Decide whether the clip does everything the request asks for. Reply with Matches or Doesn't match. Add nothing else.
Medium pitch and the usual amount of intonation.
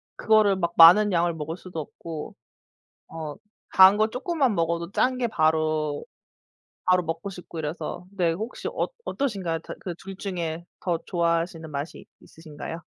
Matches